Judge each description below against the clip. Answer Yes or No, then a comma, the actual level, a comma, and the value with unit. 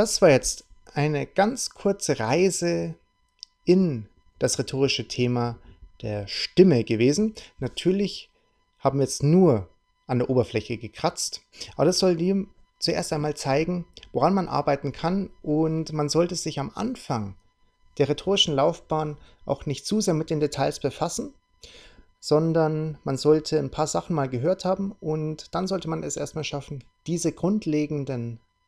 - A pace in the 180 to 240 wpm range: No, average, 145 wpm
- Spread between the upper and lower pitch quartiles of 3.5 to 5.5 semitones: Yes, average, 5.0 semitones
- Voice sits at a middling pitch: Yes, medium, 150 Hz